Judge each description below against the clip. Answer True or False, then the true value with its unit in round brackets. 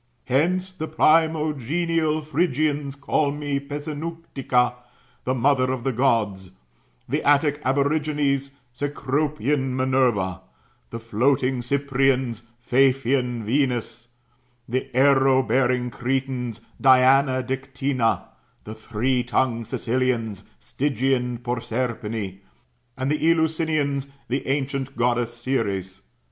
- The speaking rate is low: True (95 wpm)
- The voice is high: False (130 Hz)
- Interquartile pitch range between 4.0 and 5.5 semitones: False (2.8 semitones)